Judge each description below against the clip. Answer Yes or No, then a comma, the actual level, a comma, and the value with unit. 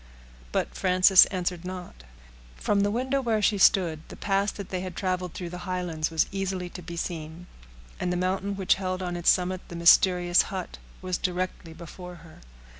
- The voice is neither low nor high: Yes, medium, 180 Hz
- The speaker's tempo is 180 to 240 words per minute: Yes, average, 185 wpm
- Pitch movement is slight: Yes, narrow, 1.6 semitones